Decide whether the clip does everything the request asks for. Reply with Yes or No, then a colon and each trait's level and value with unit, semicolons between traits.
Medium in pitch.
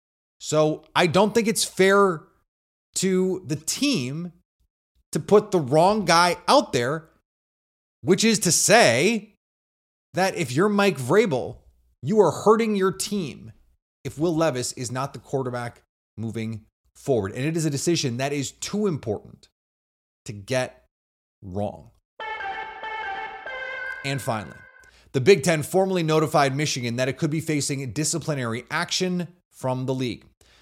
Yes: medium, 155 Hz